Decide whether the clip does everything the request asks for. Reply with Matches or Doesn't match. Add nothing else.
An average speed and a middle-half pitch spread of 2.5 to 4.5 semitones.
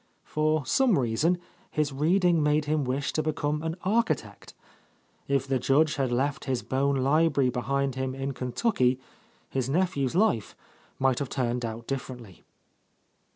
Matches